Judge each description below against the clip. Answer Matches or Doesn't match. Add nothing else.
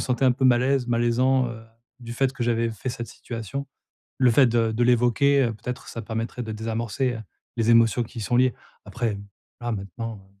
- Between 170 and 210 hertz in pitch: Doesn't match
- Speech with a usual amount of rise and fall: Doesn't match